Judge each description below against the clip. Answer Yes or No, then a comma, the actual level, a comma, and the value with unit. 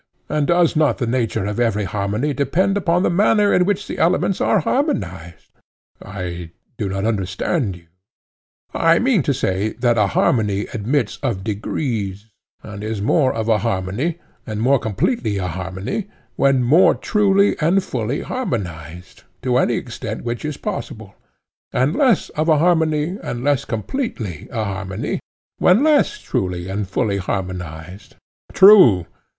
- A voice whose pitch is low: Yes, low, 115 Hz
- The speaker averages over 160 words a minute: No, average, 155 wpm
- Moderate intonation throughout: No, wide, 8.8 semitones